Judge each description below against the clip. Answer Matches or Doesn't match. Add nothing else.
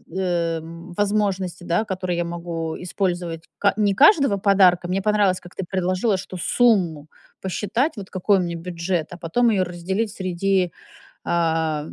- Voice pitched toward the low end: Doesn't match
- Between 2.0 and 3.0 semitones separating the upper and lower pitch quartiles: Matches